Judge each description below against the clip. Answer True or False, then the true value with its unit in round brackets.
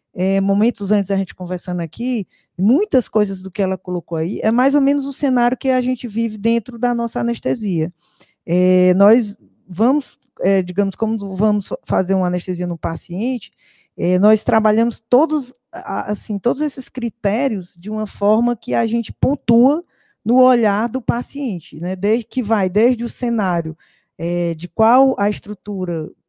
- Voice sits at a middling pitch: False (215 Hz)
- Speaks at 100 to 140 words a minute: False (160 wpm)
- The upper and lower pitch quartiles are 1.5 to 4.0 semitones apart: False (4.6 semitones)